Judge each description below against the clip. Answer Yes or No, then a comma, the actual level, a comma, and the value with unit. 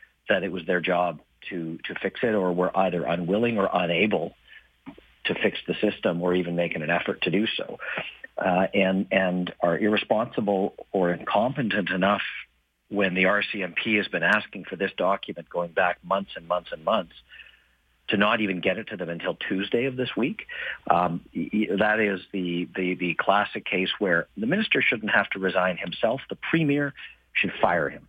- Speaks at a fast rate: No, average, 180 wpm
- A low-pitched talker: Yes, very low, 90 Hz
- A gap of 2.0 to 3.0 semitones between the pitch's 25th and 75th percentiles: Yes, narrow, 2.4 semitones